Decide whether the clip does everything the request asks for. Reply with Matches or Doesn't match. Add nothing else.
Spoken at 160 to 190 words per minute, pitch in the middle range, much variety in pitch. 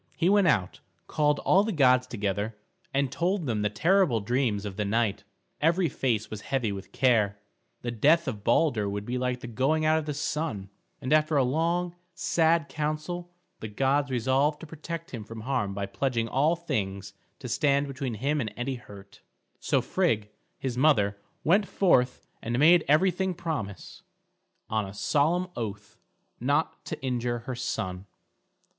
Doesn't match